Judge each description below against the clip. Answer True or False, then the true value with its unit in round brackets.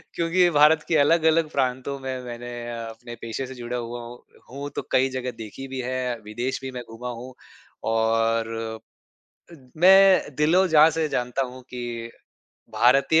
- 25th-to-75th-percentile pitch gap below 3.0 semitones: False (4.0 semitones)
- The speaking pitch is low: True (130 Hz)